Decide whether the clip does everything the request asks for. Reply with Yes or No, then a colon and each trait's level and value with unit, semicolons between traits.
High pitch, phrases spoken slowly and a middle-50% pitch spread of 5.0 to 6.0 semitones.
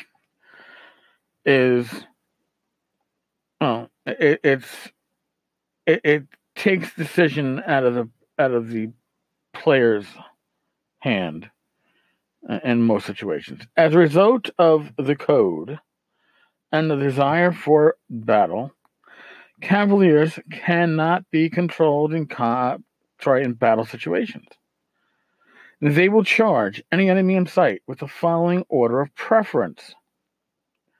No: medium, 155 Hz; slow, 105 wpm; wide, 5.4 semitones